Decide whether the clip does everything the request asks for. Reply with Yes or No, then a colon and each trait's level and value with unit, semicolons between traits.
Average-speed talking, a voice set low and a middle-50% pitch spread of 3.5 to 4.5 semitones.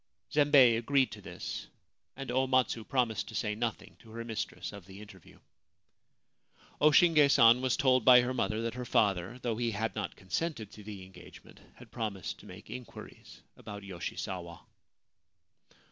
Yes: average, 160 wpm; low, 115 Hz; average, 3.8 semitones